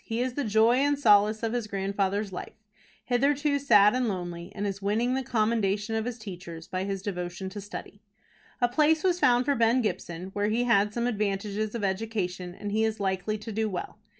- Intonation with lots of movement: No, average, 3.4 semitones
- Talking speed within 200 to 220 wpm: Yes, fast, 205 wpm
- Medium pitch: No, high, 215 Hz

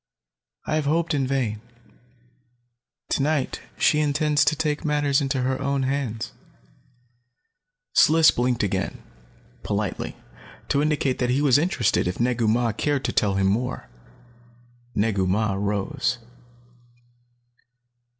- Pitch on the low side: Yes, low, 130 Hz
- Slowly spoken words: Yes, slow, 120 wpm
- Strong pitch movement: No, average, 4.9 semitones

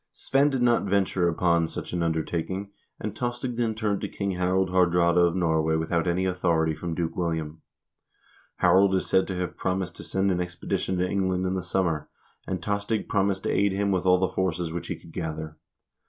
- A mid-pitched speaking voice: No, very low, 90 Hz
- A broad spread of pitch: No, narrow, 2.4 semitones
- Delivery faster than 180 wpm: Yes, average, 200 wpm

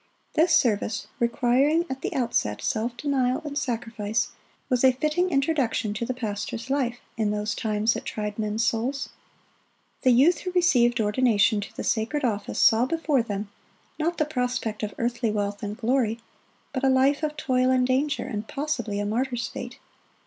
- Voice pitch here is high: Yes, high, 245 Hz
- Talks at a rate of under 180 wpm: Yes, average, 170 wpm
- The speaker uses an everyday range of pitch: Yes, average, 4.0 semitones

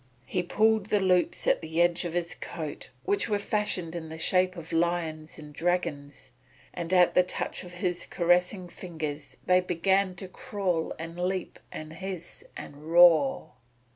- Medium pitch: Yes, medium, 175 Hz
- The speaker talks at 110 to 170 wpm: Yes, average, 165 wpm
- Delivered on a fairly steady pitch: Yes, narrow, 2.1 semitones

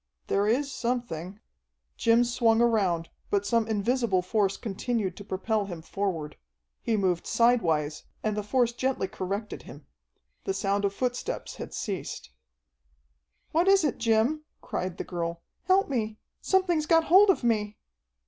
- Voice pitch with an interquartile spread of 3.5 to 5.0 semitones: Yes, average, 4.4 semitones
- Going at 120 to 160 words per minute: Yes, average, 150 wpm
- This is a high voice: Yes, high, 220 Hz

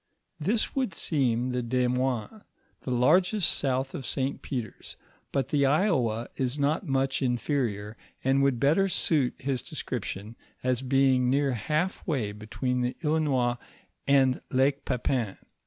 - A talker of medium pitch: No, low, 130 Hz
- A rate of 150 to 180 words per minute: No, average, 140 wpm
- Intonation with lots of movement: No, average, 2.7 semitones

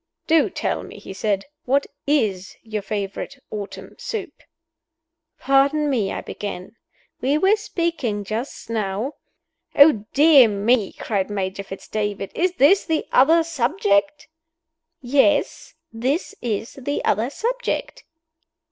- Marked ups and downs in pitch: Yes, wide, 6.6 semitones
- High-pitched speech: Yes, very high, 250 Hz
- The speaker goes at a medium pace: No, slow, 125 wpm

